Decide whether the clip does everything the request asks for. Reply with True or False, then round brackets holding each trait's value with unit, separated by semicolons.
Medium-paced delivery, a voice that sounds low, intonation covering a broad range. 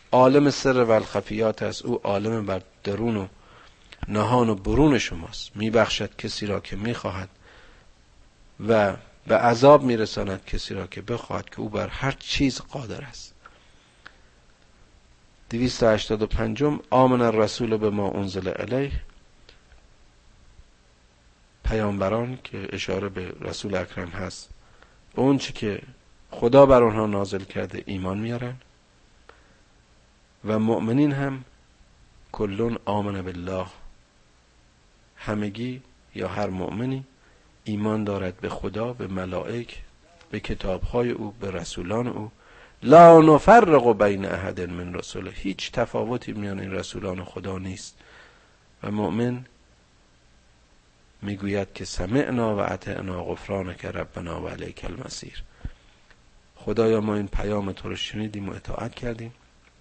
False (120 wpm; 105 Hz; 4.0 semitones)